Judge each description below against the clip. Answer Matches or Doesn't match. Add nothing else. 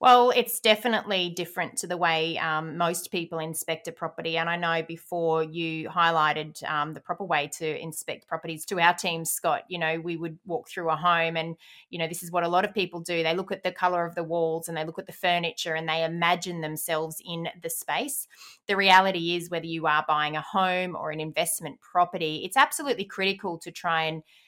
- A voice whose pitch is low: Doesn't match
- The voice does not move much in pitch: Matches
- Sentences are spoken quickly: Matches